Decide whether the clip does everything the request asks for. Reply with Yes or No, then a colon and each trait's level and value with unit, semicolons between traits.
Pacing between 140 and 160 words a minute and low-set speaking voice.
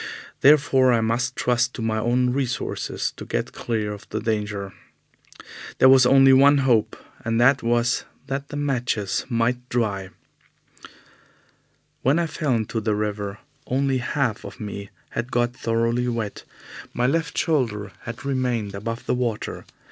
Yes: average, 150 wpm; low, 120 Hz